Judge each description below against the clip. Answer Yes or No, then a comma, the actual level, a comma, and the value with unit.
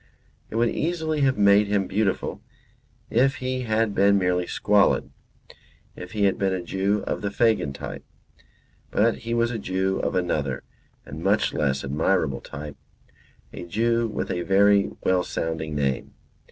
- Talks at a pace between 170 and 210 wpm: No, average, 155 wpm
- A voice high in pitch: No, low, 100 Hz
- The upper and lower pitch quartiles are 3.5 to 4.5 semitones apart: Yes, average, 4.2 semitones